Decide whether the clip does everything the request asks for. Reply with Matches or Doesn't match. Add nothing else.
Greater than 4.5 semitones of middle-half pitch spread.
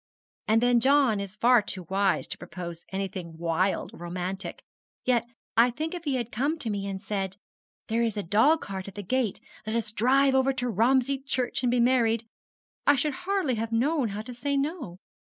Matches